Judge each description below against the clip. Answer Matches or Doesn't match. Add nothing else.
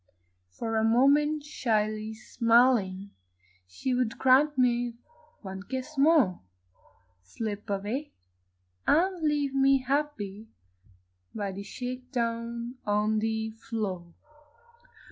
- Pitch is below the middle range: Doesn't match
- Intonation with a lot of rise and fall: Doesn't match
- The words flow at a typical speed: Doesn't match